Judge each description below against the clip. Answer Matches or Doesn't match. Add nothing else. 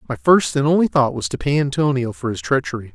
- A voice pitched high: Doesn't match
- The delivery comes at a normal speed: Doesn't match